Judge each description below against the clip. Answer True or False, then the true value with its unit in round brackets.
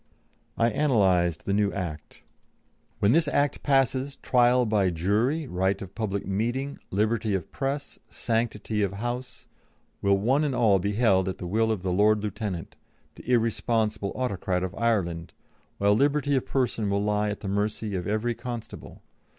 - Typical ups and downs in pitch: True (3.9 semitones)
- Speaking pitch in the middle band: False (105 Hz)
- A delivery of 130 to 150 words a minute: False (160 wpm)